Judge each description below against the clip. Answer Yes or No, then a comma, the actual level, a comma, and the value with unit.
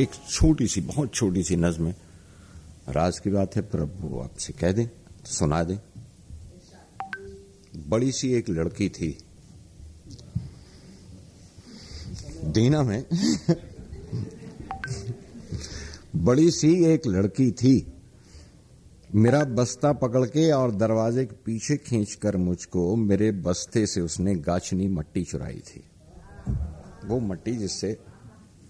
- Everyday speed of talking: No, slow, 105 wpm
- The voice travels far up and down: Yes, wide, 5.7 semitones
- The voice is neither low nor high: No, low, 105 Hz